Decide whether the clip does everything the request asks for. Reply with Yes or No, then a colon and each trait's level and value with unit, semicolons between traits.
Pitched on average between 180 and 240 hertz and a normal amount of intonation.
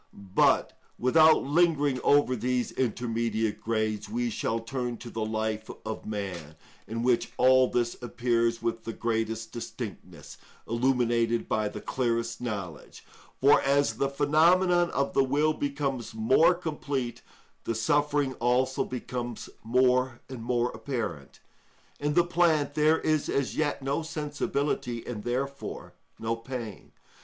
No: low, 125 Hz; average, 3.8 semitones